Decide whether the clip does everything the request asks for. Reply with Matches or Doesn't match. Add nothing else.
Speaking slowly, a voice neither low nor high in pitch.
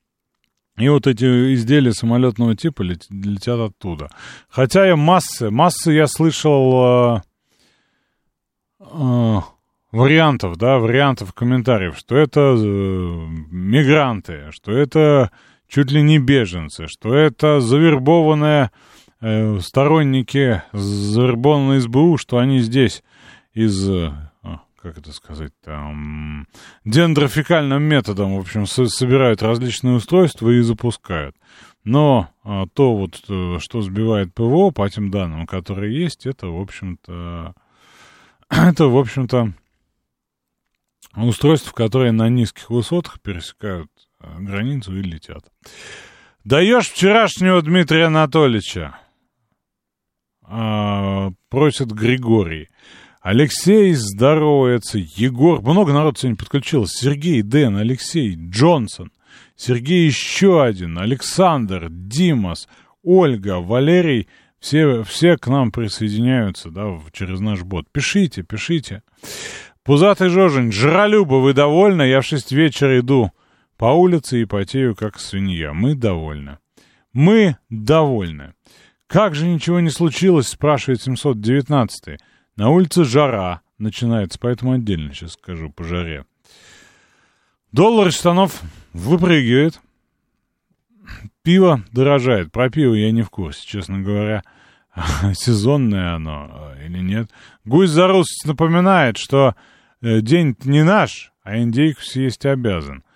Doesn't match